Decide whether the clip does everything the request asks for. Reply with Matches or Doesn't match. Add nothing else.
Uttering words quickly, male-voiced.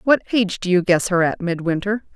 Doesn't match